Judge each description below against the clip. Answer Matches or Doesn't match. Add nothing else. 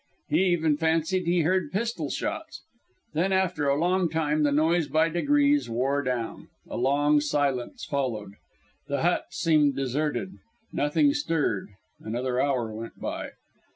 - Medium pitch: Matches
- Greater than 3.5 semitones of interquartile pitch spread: Matches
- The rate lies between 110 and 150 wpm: Matches